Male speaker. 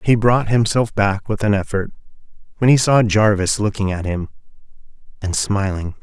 Yes: male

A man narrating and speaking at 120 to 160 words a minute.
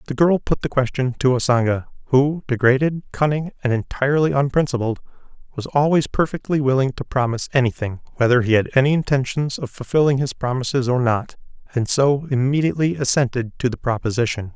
Yes: male; average, 155 wpm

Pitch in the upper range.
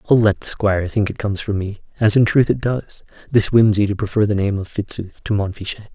No: low, 105 Hz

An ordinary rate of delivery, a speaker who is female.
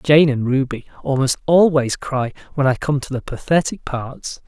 No: average, 175 wpm; male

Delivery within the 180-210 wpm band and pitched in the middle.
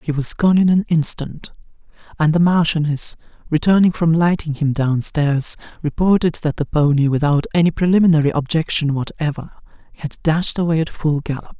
No: average, 155 wpm; medium, 155 Hz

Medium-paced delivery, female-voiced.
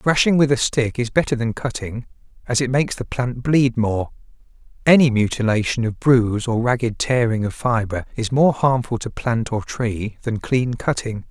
No: average, 180 wpm; male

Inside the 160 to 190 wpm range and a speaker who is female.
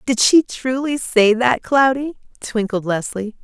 No: average, 140 wpm; female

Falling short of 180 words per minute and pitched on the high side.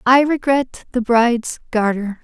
Yes: slow, 135 wpm; high, 240 Hz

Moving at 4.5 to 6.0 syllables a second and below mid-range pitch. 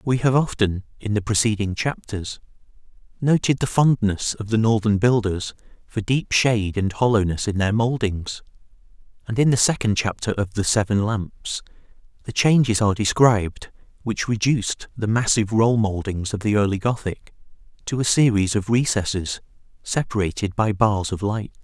Yes: 5.0 syllables/s; low, 110 Hz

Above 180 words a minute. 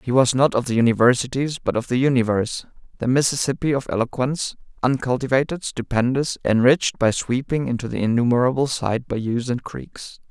No: average, 150 wpm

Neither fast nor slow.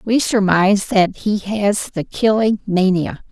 Yes: average, 145 wpm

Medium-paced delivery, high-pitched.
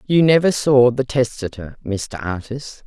No: average, 145 wpm; low, 125 Hz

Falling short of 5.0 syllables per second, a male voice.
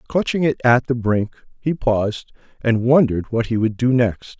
Yes: 4.7 syllables/s; male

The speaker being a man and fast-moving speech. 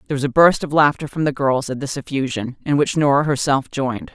No: female; fast, 245 wpm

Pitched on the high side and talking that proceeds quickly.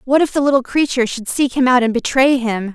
Yes: very high, 255 Hz; fast, 260 wpm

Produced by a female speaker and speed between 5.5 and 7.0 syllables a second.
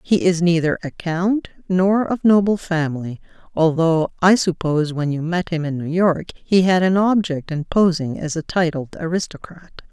No: female; 4.8 syllables/s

